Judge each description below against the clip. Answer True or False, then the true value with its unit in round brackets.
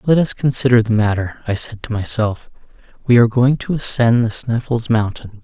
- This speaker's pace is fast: False (190 wpm)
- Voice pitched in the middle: False (115 Hz)